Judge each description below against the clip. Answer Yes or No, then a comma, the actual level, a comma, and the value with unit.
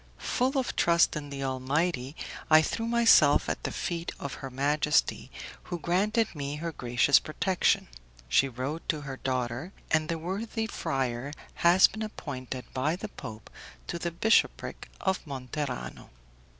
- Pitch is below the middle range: No, medium, 150 Hz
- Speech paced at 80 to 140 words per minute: No, average, 150 wpm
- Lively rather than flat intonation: No, average, 4.9 semitones